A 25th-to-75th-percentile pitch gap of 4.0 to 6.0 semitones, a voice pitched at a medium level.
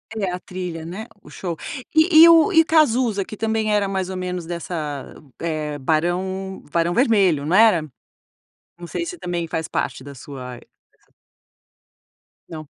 Yes: average, 5.2 semitones; medium, 180 Hz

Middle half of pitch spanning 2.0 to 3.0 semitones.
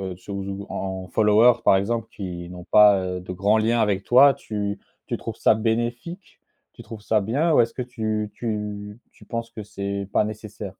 Yes: narrow, 2.6 semitones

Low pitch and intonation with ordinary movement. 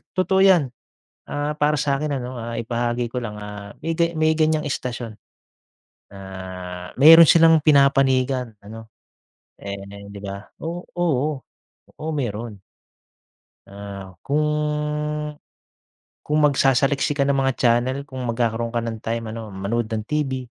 Yes: low, 125 Hz; average, 4.7 semitones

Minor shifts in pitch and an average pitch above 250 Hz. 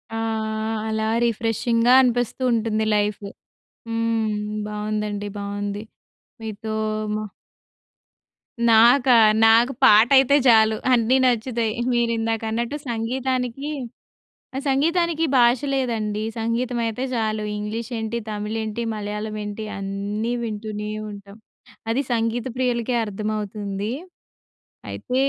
No: narrow, 2.2 semitones; high, 225 Hz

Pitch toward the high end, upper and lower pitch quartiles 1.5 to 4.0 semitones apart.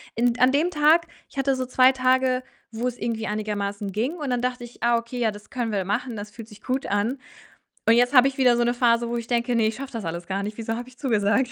Yes: high, 240 Hz; average, 2.8 semitones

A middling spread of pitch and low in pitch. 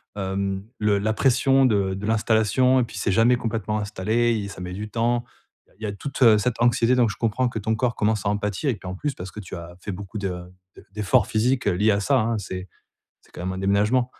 Yes: average, 3.2 semitones; low, 110 Hz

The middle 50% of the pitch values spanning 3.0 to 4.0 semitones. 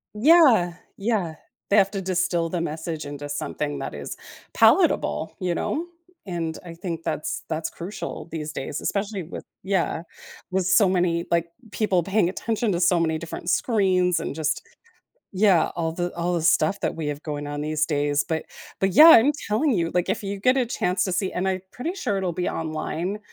Yes: average, 3.6 semitones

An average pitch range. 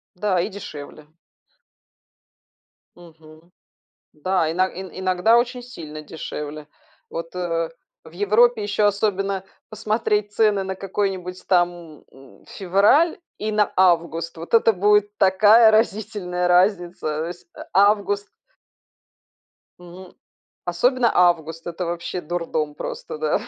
Yes: average, 3.5 semitones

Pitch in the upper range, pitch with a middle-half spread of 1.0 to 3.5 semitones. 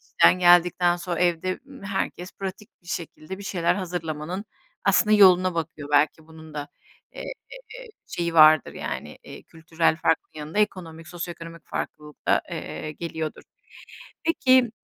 No: medium, 170 Hz; narrow, 2.6 semitones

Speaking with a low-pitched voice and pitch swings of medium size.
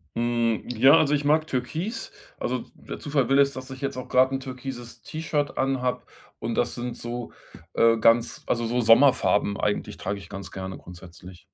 Yes: low, 125 Hz; average, 3.2 semitones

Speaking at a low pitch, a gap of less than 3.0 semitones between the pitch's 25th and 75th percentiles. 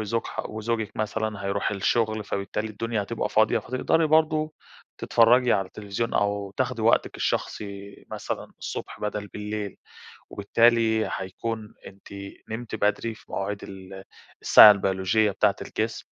Yes: low, 105 Hz; narrow, 2.4 semitones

